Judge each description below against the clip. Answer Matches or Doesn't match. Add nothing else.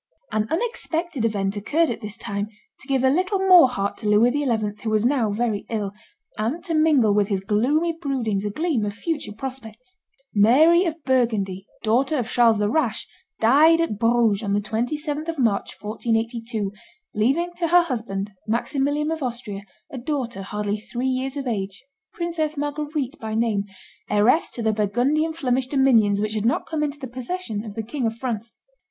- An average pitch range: Doesn't match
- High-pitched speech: Matches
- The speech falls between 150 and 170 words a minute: Doesn't match